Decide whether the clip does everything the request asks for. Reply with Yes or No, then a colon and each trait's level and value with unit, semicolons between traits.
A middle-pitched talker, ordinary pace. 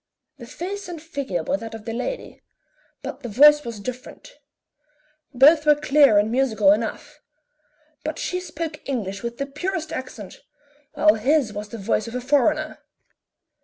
No: very high, 270 Hz; average, 160 wpm